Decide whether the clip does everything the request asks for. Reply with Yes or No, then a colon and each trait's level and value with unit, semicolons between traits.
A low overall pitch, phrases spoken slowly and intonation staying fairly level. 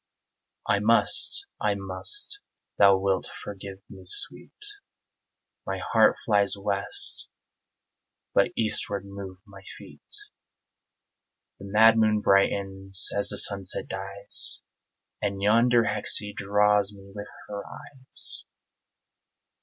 Yes: low, 100 Hz; slow, 105 wpm; narrow, 1.2 semitones